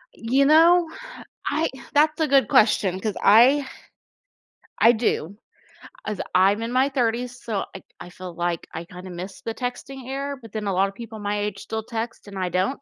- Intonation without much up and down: No, average, 5.2 semitones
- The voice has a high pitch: Yes, high, 225 Hz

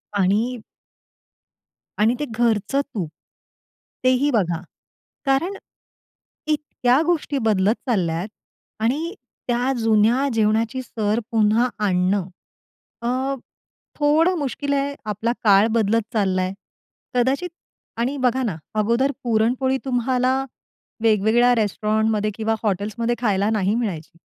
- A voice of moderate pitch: No, high, 230 Hz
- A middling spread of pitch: Yes, average, 3.7 semitones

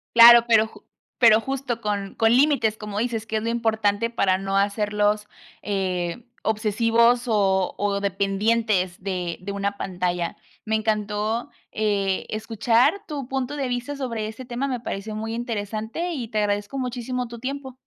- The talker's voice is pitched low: No, high, 220 Hz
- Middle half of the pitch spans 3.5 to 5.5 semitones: No, average, 2.8 semitones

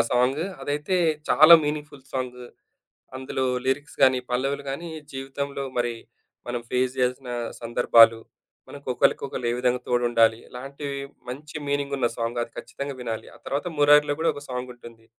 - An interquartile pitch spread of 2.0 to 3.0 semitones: Yes, narrow, 2.6 semitones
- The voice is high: No, low, 130 Hz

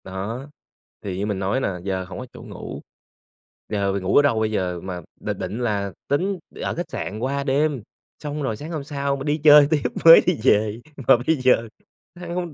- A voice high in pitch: No, low, 130 Hz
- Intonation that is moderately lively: No, wide, 6.8 semitones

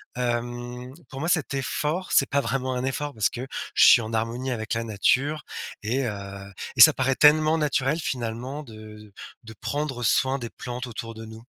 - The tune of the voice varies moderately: Yes, average, 3.4 semitones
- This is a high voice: No, low, 125 Hz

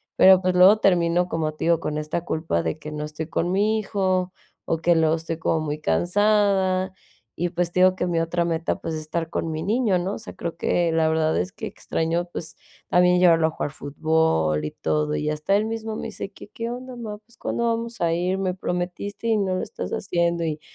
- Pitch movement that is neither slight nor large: Yes, average, 3.2 semitones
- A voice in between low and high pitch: Yes, medium, 175 Hz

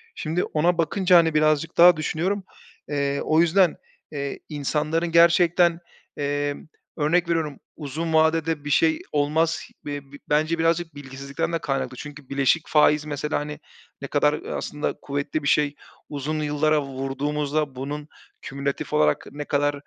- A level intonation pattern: Yes, narrow, 2.3 semitones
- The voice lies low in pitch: No, medium, 150 Hz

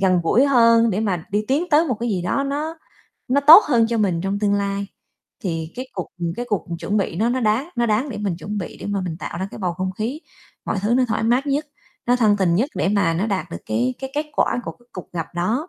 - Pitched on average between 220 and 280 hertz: No, high, 210 Hz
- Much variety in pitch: No, average, 5.0 semitones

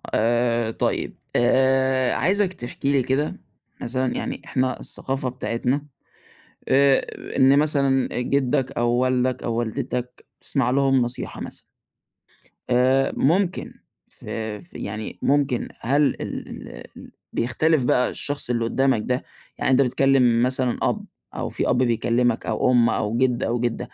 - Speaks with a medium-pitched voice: No, low, 130 Hz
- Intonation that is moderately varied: No, narrow, 2.1 semitones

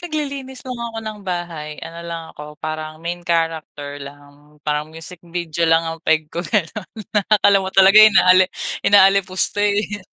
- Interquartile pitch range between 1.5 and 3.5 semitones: No, average, 4.3 semitones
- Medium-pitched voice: Yes, medium, 175 Hz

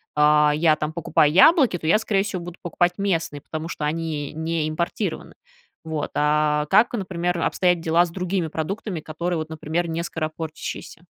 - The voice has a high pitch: No, medium, 165 Hz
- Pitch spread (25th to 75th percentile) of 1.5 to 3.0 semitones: Yes, narrow, 2.4 semitones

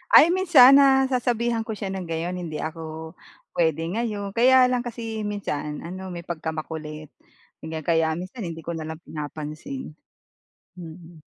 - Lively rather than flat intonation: Yes, wide, 6.6 semitones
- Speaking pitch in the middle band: Yes, medium, 175 Hz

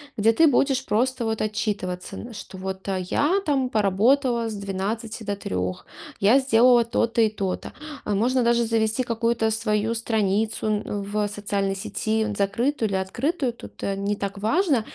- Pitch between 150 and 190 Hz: No, high, 220 Hz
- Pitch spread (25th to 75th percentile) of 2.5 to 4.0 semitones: Yes, average, 2.9 semitones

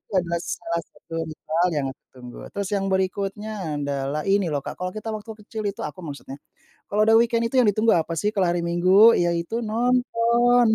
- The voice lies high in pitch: Yes, high, 195 Hz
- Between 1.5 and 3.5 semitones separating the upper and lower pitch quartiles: No, average, 4.8 semitones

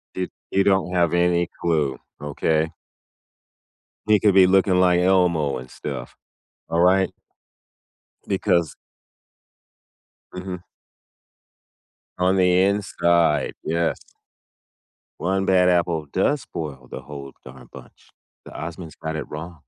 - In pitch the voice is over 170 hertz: No, very low, 85 Hz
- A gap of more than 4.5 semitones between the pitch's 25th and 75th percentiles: No, average, 2.9 semitones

